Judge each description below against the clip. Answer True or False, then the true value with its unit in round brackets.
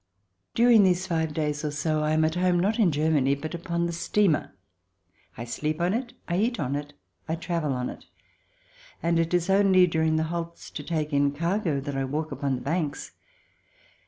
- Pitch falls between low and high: True (160 Hz)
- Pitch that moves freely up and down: False (3.1 semitones)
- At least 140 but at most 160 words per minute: False (195 wpm)